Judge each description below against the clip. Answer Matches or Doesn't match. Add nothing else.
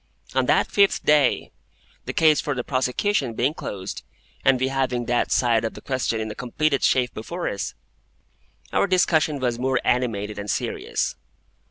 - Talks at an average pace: Matches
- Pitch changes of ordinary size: Matches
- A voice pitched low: Matches